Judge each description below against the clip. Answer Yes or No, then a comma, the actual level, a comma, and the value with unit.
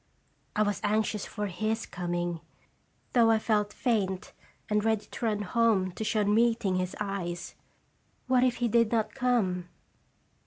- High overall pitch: Yes, high, 210 Hz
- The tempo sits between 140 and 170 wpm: Yes, average, 150 wpm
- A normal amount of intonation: Yes, average, 3.2 semitones